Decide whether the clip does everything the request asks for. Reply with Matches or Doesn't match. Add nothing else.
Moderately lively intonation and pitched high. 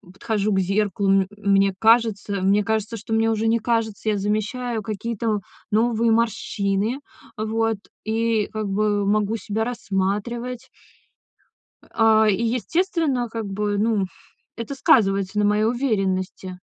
Doesn't match